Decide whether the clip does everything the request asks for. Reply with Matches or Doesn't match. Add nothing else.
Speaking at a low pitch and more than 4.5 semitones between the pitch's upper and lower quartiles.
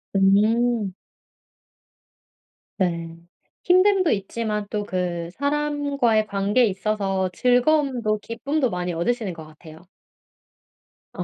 Doesn't match